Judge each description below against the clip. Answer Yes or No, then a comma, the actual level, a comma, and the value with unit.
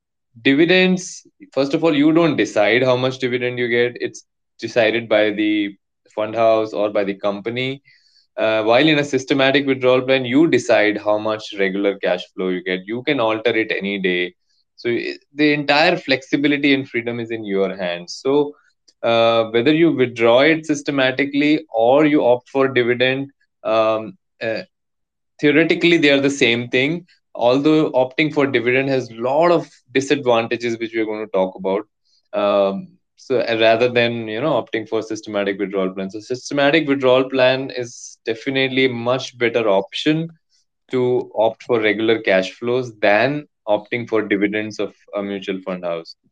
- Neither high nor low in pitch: No, low, 125 Hz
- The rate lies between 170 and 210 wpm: No, average, 160 wpm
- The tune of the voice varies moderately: Yes, average, 4.8 semitones